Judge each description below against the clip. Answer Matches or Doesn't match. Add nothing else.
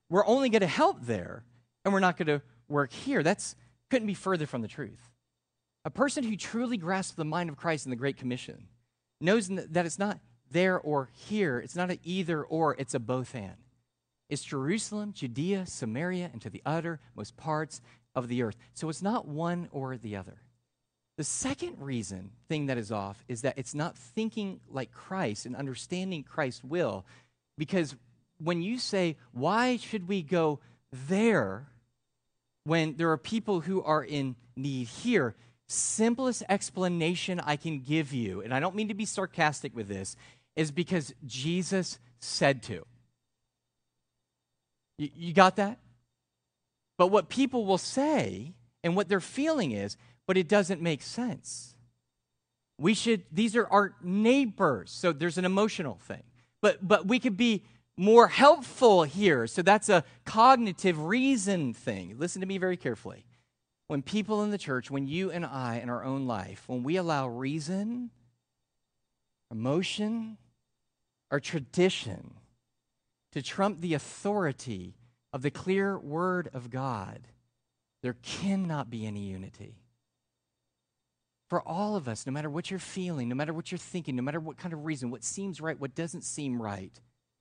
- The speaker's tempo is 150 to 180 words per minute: Matches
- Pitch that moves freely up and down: Matches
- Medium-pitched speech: Matches